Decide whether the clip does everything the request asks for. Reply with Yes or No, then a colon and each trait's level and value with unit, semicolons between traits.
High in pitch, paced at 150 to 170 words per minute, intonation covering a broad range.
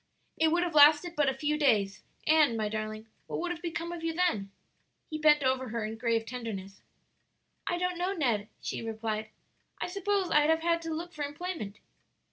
No: very high, 295 Hz; average, 195 wpm; wide, 7.2 semitones